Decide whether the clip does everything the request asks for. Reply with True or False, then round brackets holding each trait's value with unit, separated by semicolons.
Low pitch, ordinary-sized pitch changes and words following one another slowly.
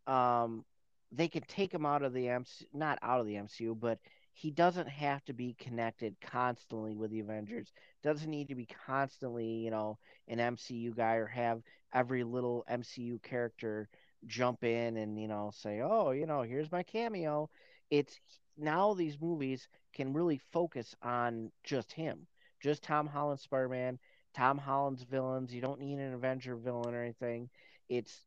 False (125 Hz; 3.7 semitones; 170 wpm)